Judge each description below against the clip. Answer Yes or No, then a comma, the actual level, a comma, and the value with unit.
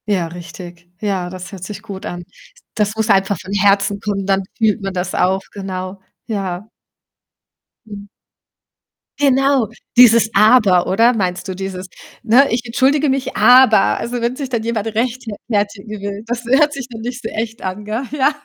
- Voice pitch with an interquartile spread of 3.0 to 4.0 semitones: Yes, average, 3.7 semitones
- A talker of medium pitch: No, high, 210 Hz